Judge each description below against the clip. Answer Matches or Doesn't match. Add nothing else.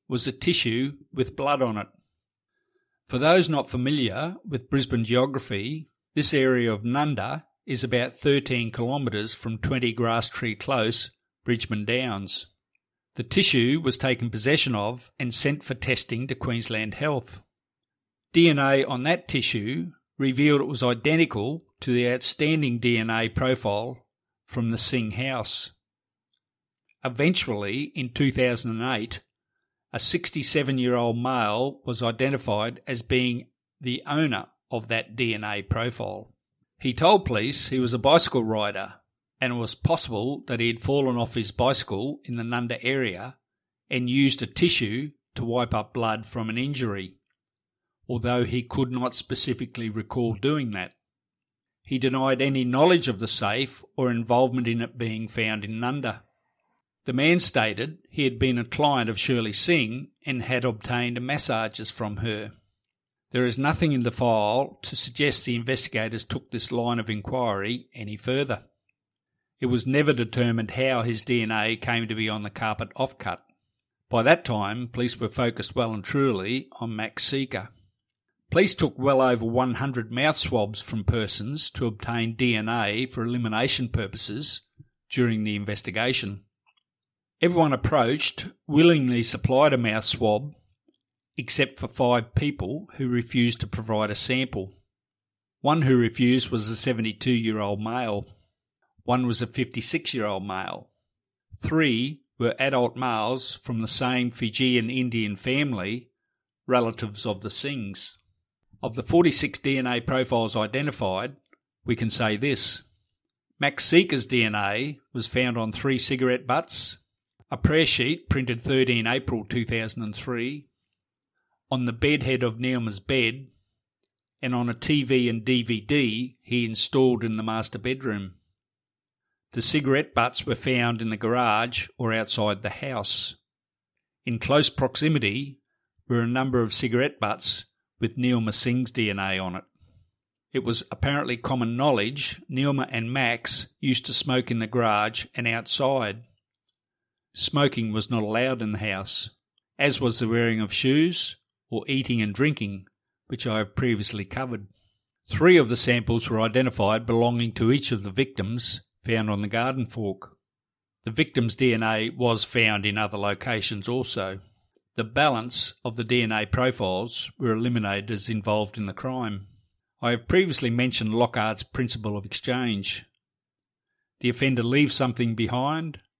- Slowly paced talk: Doesn't match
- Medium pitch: Doesn't match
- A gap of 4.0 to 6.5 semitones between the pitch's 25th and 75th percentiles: Doesn't match